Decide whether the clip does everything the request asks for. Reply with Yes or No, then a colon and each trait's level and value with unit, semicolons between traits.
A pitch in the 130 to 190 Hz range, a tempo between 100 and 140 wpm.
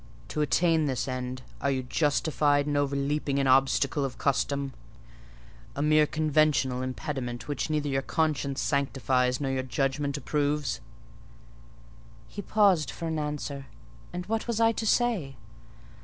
Yes: medium, 140 Hz; slow, 135 wpm